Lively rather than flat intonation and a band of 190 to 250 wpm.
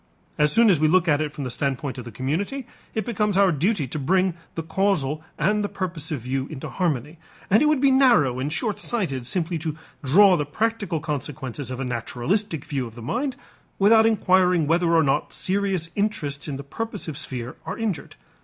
Yes: wide, 6.4 semitones; average, 200 wpm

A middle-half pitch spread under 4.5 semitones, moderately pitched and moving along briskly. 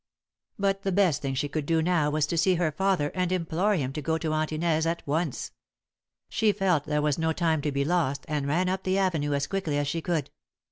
Yes: average, 3.6 semitones; medium, 160 Hz; fast, 235 wpm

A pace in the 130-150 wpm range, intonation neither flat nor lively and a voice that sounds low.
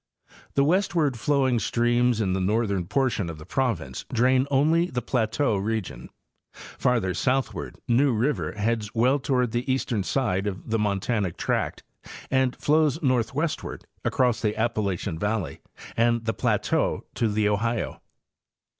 Yes: average, 145 wpm; average, 4.0 semitones; low, 115 Hz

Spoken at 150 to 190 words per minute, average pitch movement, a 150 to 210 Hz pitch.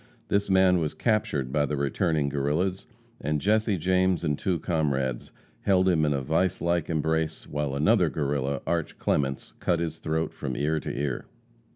No: average, 170 wpm; average, 4.0 semitones; very low, 80 Hz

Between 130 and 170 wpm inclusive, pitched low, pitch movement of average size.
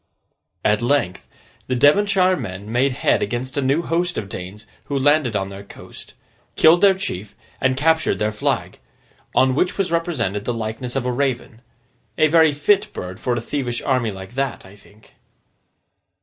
No: average, 165 wpm; low, 130 Hz; wide, 6.4 semitones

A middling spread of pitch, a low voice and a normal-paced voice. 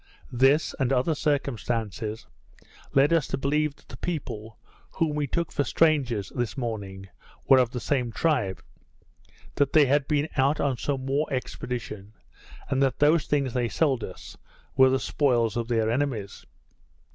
Yes: average, 3.8 semitones; low, 130 Hz; average, 155 wpm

